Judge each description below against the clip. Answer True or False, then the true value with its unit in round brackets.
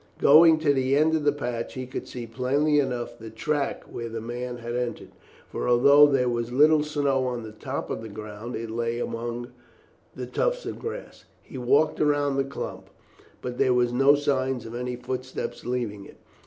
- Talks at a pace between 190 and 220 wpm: True (195 wpm)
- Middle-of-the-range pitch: False (125 Hz)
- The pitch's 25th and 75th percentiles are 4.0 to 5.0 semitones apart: False (3.3 semitones)